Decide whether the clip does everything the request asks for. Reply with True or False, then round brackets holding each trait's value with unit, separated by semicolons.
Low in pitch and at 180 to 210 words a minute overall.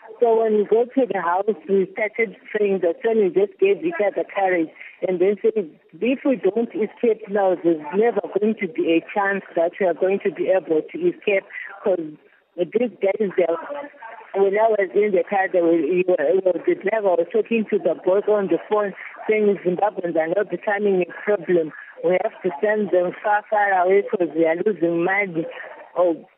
False (195 Hz; 200 wpm)